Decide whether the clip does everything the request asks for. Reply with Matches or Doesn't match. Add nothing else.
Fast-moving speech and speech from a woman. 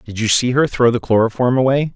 Doesn't match